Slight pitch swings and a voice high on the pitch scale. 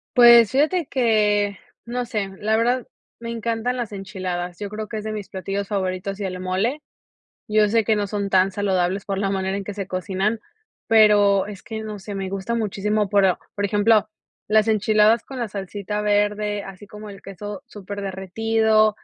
Yes: narrow, 2.0 semitones; high, 205 Hz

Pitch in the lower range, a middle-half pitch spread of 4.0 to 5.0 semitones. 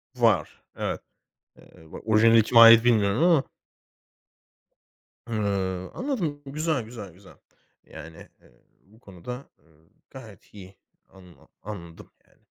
Yes: low, 110 Hz; average, 4.6 semitones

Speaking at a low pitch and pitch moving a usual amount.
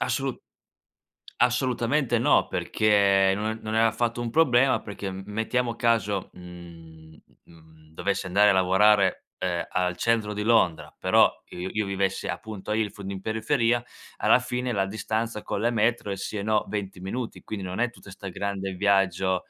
Yes: low, 105 Hz; average, 3.4 semitones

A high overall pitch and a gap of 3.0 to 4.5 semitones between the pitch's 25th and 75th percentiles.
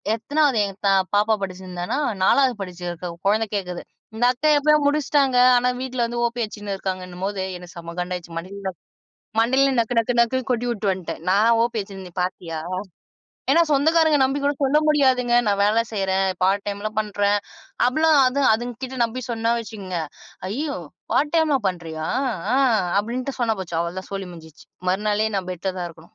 No: high, 215 Hz; wide, 5.4 semitones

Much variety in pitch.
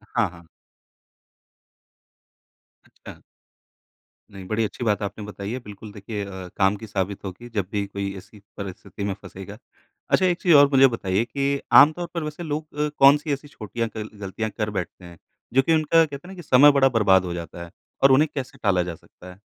Yes: wide, 6.2 semitones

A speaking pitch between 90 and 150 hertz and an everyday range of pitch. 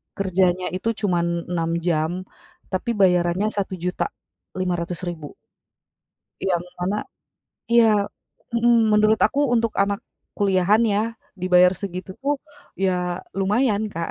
No: high, 190 Hz; average, 3.0 semitones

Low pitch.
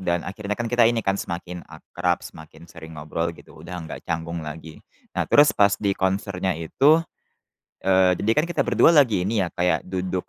Yes: very low, 95 Hz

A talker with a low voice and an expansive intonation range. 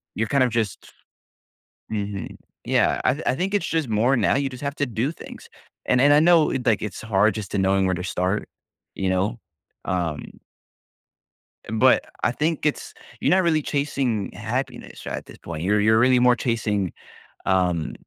Yes: low, 115 Hz; wide, 6.1 semitones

